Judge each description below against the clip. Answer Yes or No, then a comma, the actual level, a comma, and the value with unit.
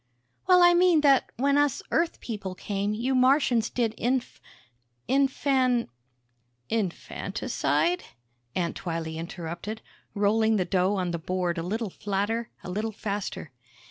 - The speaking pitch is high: Yes, high, 215 Hz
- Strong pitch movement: Yes, wide, 6.2 semitones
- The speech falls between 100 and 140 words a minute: Yes, slow, 135 wpm